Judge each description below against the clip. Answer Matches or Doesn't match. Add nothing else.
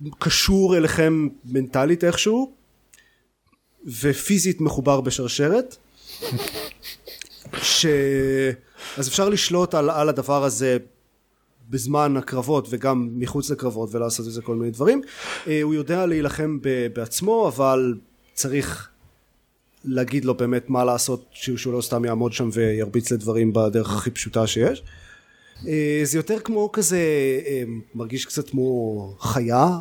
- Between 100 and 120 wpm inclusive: Matches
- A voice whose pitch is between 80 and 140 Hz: Matches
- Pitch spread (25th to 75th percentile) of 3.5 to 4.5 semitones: Matches